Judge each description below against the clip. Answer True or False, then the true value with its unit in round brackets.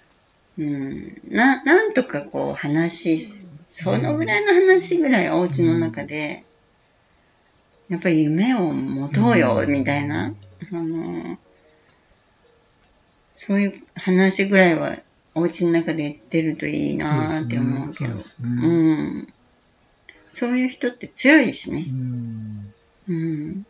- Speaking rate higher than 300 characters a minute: False (215 characters per minute)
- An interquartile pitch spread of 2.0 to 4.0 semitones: False (5.2 semitones)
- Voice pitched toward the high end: False (165 Hz)